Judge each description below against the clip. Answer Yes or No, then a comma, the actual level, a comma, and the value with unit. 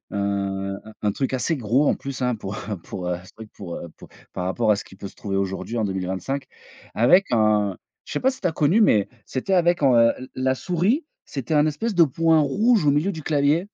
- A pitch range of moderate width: No, wide, 8.0 semitones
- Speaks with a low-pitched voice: Yes, low, 130 Hz